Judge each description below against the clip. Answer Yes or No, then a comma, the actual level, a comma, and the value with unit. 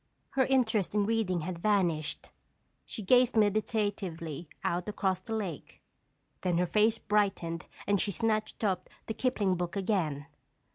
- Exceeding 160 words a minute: No, average, 140 wpm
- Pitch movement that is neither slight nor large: Yes, average, 3.7 semitones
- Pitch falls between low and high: No, high, 200 Hz